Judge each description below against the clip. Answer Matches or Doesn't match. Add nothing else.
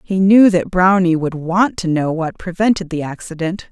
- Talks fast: Doesn't match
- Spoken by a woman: Matches